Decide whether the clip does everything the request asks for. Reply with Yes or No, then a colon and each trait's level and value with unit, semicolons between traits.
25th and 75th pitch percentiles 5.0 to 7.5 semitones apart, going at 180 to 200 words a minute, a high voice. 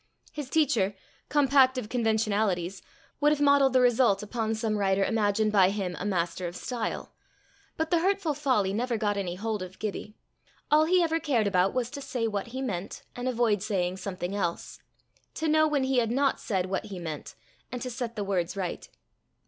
Yes: average, 5.3 semitones; average, 190 wpm; high, 220 Hz